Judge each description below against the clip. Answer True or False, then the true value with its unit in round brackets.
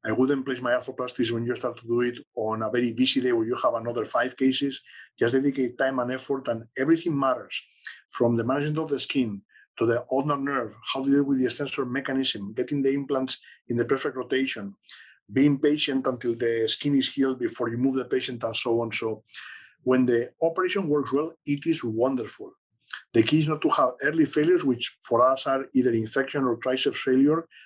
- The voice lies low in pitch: True (130 Hz)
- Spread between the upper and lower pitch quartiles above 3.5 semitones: False (2.8 semitones)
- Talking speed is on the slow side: False (205 wpm)